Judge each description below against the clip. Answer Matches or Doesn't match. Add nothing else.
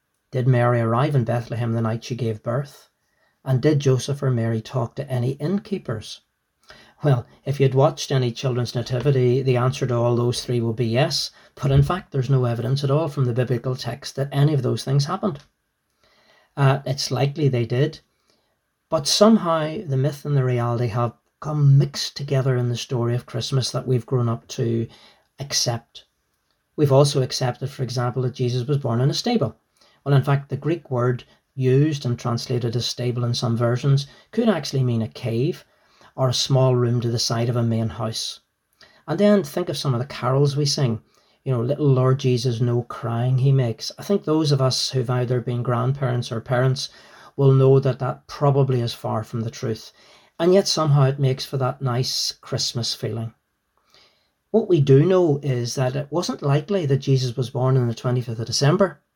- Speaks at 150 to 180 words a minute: Doesn't match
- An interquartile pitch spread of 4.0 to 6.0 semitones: Doesn't match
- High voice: Doesn't match